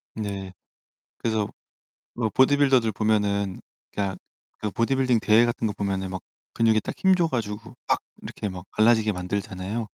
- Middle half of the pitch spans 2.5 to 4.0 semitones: Yes, average, 2.9 semitones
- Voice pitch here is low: Yes, low, 110 Hz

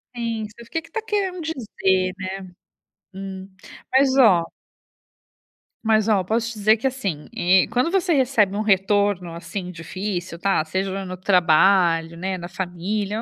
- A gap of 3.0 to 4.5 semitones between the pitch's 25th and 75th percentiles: Yes, average, 4.1 semitones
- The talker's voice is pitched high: Yes, high, 195 Hz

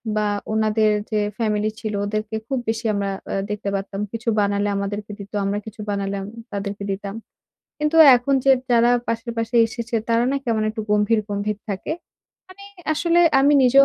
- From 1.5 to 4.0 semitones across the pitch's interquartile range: Yes, narrow, 2.5 semitones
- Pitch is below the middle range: No, high, 215 Hz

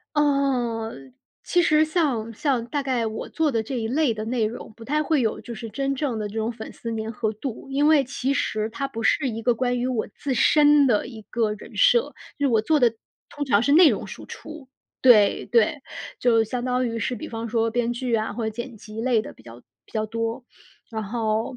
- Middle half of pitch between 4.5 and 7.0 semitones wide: No, average, 3.7 semitones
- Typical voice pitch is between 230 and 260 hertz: Yes, high, 240 Hz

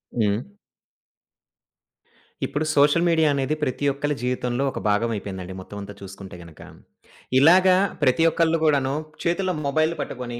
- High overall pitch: No, low, 135 Hz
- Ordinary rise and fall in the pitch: No, wide, 7.1 semitones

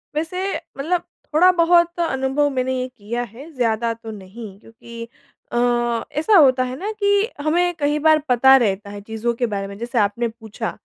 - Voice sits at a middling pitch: No, very high, 255 Hz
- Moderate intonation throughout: No, wide, 6.2 semitones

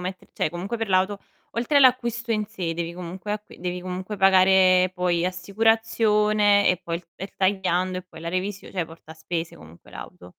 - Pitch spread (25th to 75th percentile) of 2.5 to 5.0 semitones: Yes, average, 2.9 semitones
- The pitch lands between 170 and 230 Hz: Yes, medium, 185 Hz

